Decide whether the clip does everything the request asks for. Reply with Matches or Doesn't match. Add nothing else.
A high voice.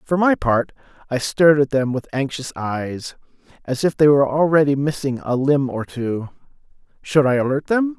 Doesn't match